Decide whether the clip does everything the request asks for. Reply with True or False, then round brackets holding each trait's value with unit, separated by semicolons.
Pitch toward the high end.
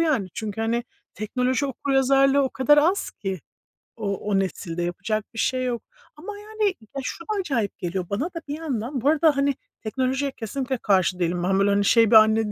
True (240 Hz)